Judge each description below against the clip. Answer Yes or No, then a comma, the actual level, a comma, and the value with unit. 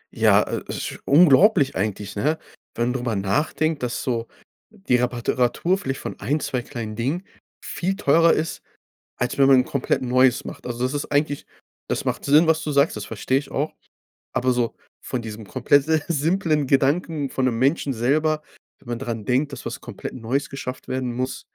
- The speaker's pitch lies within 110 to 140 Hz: Yes, low, 135 Hz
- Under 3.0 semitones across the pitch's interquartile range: No, average, 3.7 semitones